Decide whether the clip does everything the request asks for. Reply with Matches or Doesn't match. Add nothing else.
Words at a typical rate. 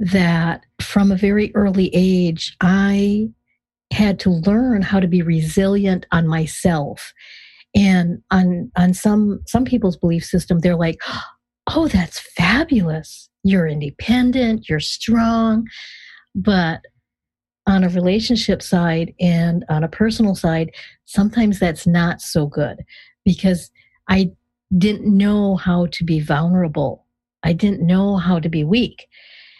Doesn't match